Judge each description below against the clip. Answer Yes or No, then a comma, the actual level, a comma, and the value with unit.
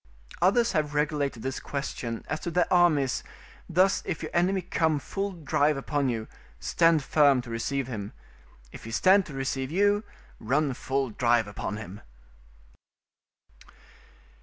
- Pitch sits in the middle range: Yes, medium, 145 Hz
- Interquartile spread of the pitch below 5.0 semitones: No, average, 5.3 semitones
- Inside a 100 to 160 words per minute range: Yes, average, 140 wpm